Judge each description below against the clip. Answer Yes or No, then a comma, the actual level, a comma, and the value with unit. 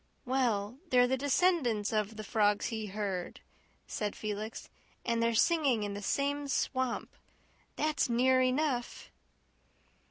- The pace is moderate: No, slow, 125 wpm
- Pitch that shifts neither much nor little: Yes, average, 3.8 semitones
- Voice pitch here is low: No, high, 235 Hz